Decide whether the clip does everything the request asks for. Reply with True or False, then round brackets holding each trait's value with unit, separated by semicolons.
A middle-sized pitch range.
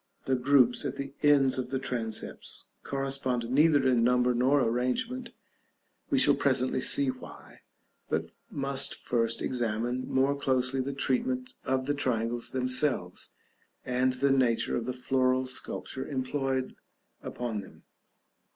False (1.7 semitones)